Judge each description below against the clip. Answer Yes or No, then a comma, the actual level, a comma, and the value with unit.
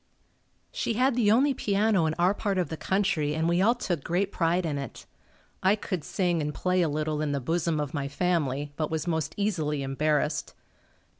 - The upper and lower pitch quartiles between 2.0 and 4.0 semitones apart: No, average, 4.6 semitones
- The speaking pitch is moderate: Yes, medium, 165 Hz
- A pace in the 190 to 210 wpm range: Yes, average, 200 wpm